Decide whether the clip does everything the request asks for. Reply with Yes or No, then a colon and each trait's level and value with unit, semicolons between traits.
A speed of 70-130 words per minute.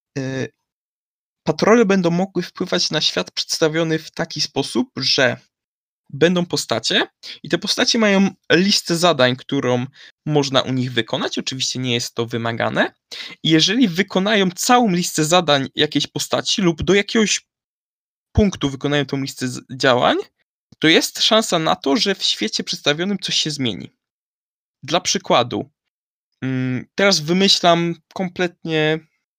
Yes: average, 125 wpm